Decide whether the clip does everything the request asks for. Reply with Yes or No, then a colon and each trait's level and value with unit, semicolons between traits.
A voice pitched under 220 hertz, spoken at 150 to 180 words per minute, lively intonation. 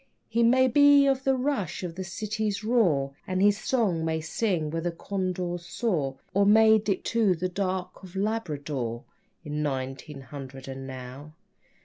Yes: medium, 185 Hz; average, 160 wpm; wide, 6.6 semitones